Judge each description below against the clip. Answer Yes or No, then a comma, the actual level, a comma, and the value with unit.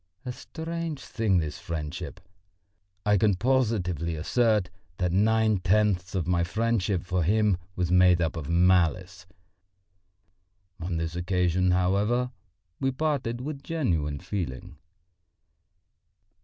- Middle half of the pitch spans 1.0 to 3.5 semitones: No, average, 4.4 semitones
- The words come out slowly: Yes, slow, 115 wpm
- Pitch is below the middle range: Yes, very low, 95 Hz